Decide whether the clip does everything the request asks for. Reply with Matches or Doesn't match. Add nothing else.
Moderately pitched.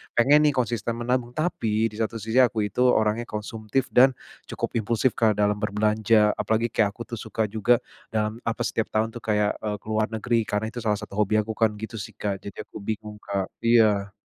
Doesn't match